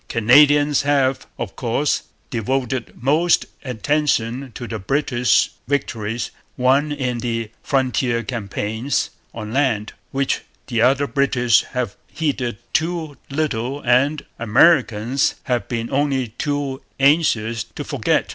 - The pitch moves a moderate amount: Yes, average, 3.5 semitones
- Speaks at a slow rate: Yes, slow, 115 wpm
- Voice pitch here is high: No, low, 130 Hz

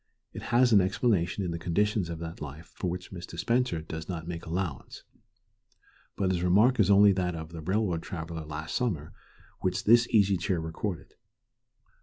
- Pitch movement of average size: Yes, average, 3.7 semitones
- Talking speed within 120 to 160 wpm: No, average, 175 wpm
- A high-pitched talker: No, very low, 90 Hz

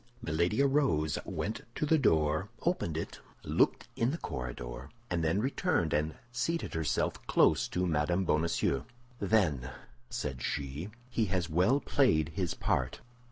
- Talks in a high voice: No, very low, 85 Hz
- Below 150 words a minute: Yes, average, 140 wpm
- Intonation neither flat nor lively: No, wide, 7.1 semitones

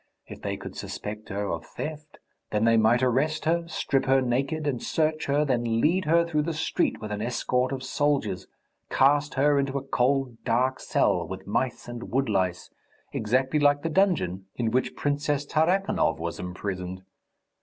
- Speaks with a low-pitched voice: Yes, low, 130 Hz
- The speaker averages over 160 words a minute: Yes, average, 170 wpm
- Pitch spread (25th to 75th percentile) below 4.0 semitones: No, average, 5.2 semitones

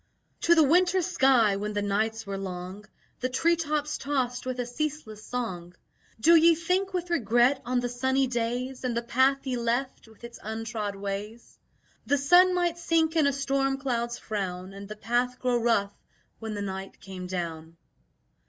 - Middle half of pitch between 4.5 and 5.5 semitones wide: Yes, average, 5.1 semitones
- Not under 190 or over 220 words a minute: No, average, 175 wpm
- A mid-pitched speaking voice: No, high, 245 Hz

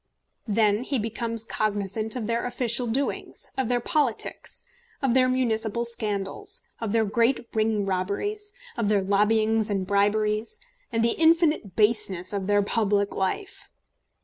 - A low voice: No, high, 220 Hz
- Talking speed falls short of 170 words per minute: Yes, average, 140 wpm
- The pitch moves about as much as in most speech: Yes, average, 3.0 semitones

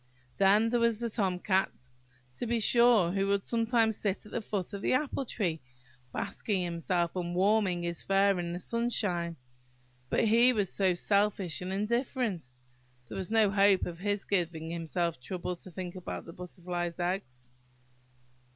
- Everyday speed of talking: Yes, average, 160 wpm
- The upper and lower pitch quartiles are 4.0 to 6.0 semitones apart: No, average, 3.6 semitones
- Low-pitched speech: No, high, 190 Hz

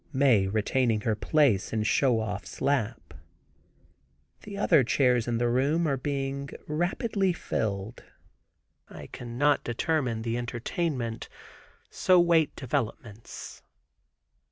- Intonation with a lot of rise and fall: No, average, 4.6 semitones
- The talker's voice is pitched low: Yes, low, 125 Hz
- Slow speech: Yes, slow, 110 wpm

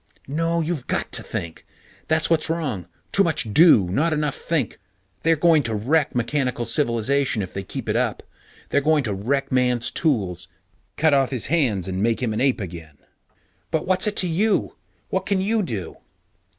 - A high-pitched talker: No, low, 135 Hz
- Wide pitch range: Yes, wide, 6.9 semitones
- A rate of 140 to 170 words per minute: No, average, 185 wpm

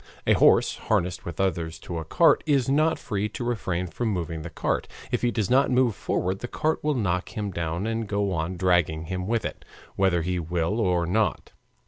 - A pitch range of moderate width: Yes, average, 4.9 semitones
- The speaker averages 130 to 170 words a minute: No, fast, 205 wpm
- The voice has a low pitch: Yes, very low, 95 Hz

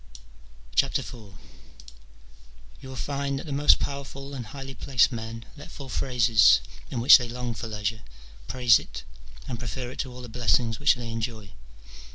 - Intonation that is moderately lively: Yes, average, 3.0 semitones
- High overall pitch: No, low, 125 Hz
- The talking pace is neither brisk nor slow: Yes, average, 165 wpm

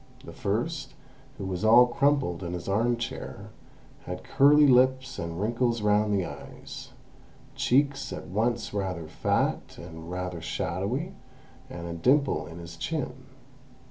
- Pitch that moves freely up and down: Yes, wide, 6.6 semitones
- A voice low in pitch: Yes, low, 105 Hz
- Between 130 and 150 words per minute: Yes, average, 140 wpm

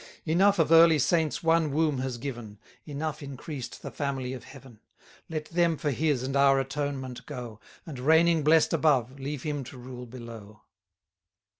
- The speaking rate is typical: Yes, average, 160 wpm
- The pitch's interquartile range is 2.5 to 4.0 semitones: Yes, average, 3.7 semitones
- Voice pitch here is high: No, medium, 140 Hz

